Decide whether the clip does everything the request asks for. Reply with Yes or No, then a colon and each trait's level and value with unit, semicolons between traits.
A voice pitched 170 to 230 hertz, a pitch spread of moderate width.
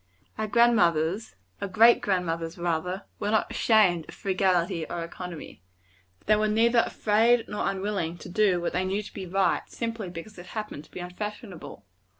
Yes: high, 190 Hz; average, 3.6 semitones